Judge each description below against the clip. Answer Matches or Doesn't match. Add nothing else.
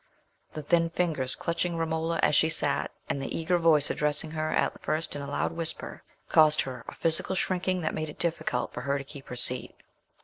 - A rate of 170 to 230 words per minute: Matches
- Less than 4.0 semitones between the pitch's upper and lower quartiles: Matches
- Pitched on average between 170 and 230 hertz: Doesn't match